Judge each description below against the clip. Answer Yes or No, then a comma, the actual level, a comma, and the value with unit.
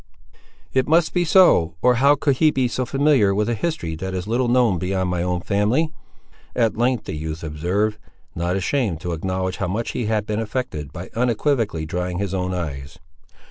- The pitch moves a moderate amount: No, wide, 6.0 semitones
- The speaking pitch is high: No, low, 105 Hz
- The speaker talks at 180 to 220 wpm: Yes, average, 190 wpm